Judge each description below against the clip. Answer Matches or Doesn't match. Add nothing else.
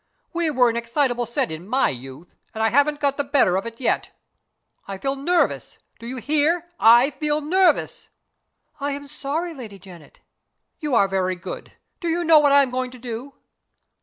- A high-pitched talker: Matches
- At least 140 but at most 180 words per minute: Doesn't match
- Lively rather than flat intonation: Doesn't match